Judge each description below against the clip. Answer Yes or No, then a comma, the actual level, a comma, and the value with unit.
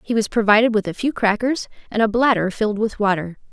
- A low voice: No, high, 215 Hz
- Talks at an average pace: No, fast, 220 wpm